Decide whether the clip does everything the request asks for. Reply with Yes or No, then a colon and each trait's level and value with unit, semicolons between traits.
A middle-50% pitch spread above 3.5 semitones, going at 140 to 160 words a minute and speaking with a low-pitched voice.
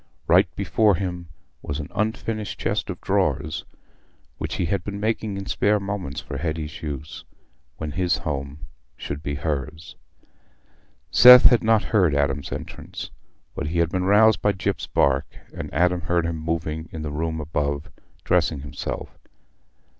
Yes: average, 5.0 semitones; average, 155 wpm; very low, 80 Hz